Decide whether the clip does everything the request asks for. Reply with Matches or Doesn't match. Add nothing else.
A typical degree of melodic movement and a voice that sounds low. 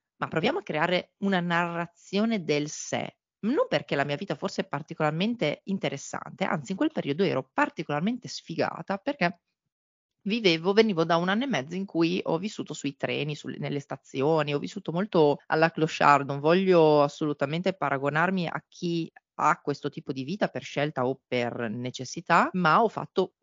Doesn't match